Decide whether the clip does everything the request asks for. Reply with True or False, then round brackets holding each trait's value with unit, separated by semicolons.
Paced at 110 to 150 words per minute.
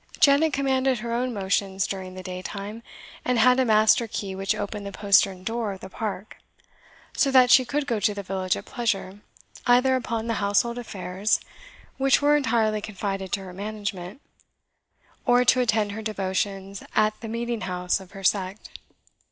False (170 wpm)